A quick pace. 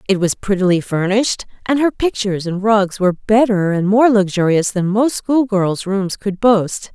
No: average, 175 wpm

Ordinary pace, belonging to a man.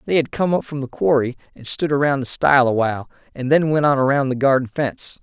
No: fast, 255 wpm; male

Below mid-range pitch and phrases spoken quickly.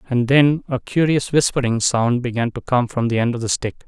Yes: low, 125 Hz; fast, 230 wpm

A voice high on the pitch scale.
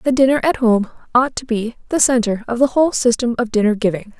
Yes: high, 240 Hz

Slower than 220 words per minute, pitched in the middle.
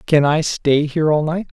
No: fast, 230 wpm; medium, 155 Hz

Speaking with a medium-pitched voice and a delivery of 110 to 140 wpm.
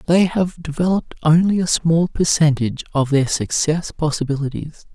Yes: medium, 160 Hz; slow, 135 wpm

